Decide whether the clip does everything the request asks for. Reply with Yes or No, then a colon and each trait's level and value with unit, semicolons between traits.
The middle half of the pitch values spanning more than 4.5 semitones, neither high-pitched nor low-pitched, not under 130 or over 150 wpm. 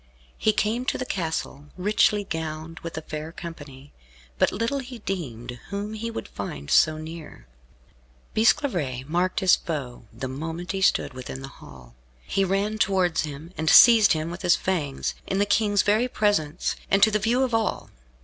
No: wide, 5.4 semitones; medium, 175 Hz; average, 175 wpm